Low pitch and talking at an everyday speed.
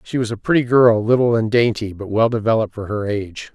No: low, 110 Hz; fast, 235 wpm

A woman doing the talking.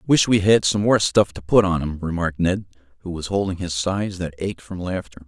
No: male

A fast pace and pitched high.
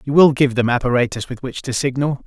No: fast, 240 wpm; low, 130 Hz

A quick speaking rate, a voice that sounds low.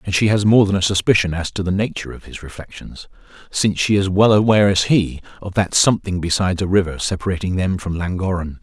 Yes: fast, 215 wpm; very low, 95 Hz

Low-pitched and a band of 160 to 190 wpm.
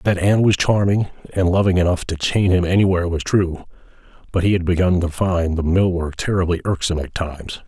No: very low, 90 Hz; fast, 205 wpm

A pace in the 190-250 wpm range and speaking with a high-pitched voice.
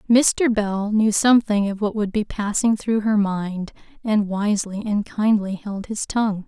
No: average, 175 wpm; high, 210 Hz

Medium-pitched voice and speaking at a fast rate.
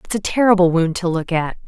Yes: medium, 180 Hz; fast, 250 wpm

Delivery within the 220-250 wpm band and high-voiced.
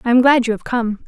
No: fast, 335 wpm; high, 240 Hz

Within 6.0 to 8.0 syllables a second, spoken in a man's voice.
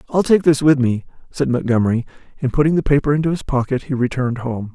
Yes: 6.5 syllables/s; male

